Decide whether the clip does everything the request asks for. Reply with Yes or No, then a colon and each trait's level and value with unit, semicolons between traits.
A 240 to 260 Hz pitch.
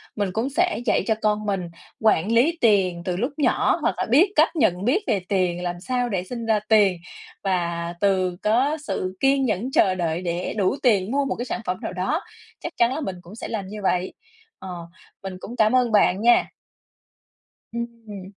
No: high, 210 Hz